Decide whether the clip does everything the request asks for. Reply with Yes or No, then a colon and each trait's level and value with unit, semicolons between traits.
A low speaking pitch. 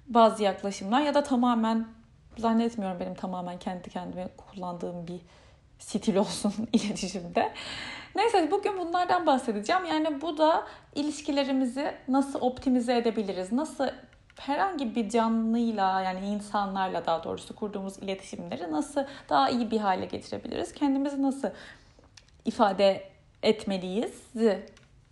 No: high, 225 Hz